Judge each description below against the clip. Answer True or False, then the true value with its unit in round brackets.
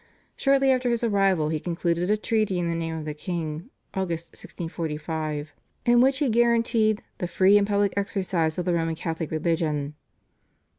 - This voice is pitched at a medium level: True (175 Hz)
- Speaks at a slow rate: False (165 wpm)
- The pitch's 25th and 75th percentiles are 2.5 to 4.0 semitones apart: False (4.9 semitones)